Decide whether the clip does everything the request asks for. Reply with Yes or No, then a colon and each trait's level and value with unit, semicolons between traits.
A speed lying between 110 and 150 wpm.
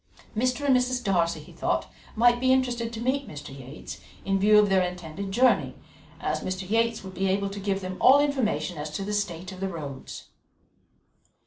No: average, 195 wpm